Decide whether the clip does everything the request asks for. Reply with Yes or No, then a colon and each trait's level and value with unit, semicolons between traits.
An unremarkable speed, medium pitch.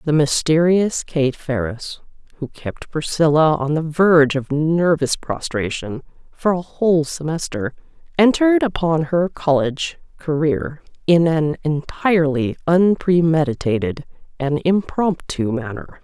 No: slow, 110 wpm; medium, 155 Hz